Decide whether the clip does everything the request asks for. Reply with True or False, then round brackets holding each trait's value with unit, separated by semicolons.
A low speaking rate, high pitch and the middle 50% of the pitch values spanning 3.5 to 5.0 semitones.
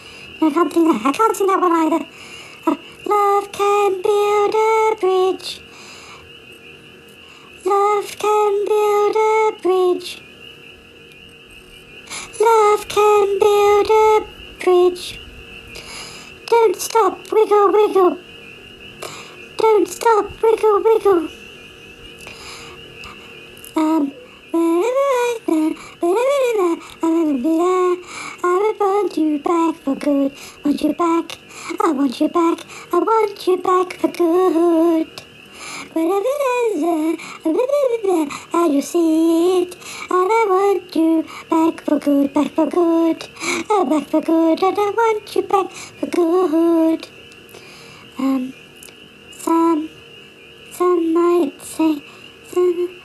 True (105 wpm; 360 Hz; 4.0 semitones)